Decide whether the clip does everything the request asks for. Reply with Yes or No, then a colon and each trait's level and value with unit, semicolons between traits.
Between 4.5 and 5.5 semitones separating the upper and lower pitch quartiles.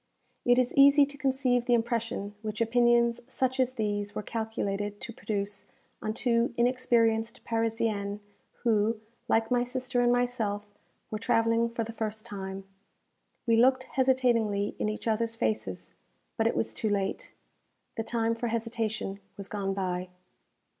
No: narrow, 2.4 semitones